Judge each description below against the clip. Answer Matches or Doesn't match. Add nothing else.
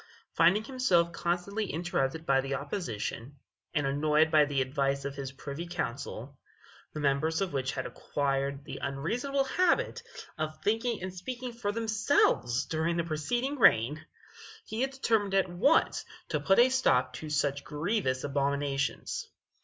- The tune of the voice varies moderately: Doesn't match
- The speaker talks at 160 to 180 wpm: Doesn't match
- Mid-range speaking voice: Matches